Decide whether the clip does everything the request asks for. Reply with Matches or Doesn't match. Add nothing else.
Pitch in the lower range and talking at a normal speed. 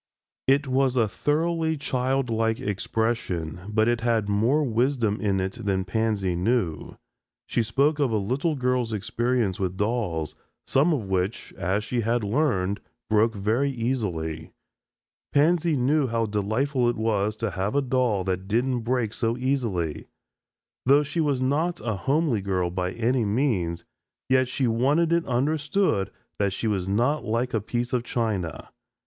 Matches